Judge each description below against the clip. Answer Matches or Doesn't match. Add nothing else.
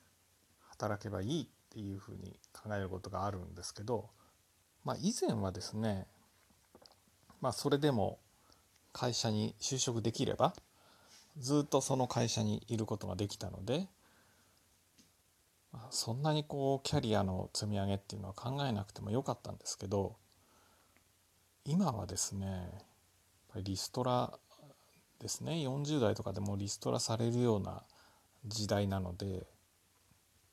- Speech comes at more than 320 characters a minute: Doesn't match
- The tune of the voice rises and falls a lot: Doesn't match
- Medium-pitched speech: Doesn't match